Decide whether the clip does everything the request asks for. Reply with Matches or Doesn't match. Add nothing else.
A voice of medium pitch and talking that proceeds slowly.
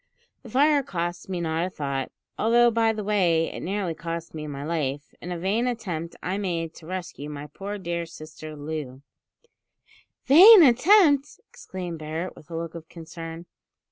Doesn't match